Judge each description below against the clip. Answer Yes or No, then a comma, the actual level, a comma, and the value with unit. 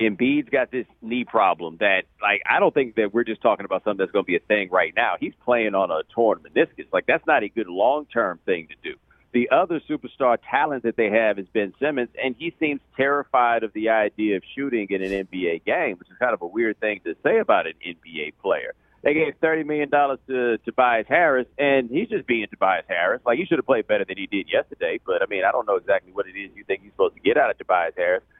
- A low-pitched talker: Yes, low, 125 Hz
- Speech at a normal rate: No, fast, 250 wpm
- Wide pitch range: Yes, wide, 6.6 semitones